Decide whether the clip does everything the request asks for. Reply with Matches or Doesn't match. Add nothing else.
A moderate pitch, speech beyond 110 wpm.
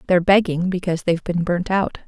Matches